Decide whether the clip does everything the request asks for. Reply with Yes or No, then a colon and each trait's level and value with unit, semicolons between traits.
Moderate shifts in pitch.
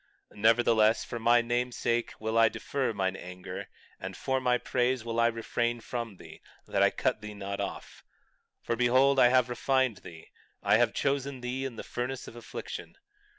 No: narrow, 2.3 semitones